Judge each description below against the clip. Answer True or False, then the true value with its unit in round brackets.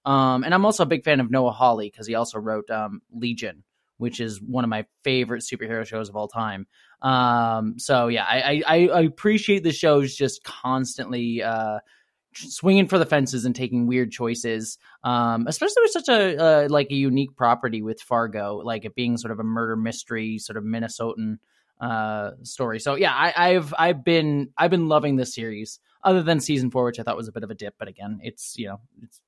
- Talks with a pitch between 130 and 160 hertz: False (120 Hz)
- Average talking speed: False (210 wpm)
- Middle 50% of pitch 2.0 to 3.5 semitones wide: False (4.4 semitones)